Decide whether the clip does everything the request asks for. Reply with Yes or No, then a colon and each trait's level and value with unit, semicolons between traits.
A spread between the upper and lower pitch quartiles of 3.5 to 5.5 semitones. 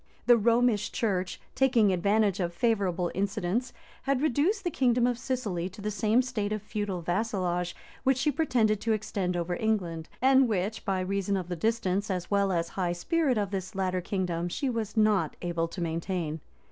Yes: average, 4.3 semitones